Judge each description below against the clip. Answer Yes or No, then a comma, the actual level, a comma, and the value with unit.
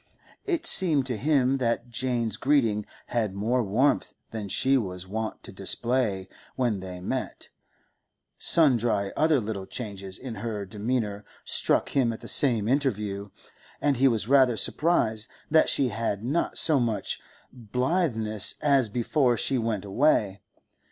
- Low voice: Yes, low, 115 Hz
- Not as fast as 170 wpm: Yes, average, 140 wpm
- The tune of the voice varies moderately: Yes, average, 4.3 semitones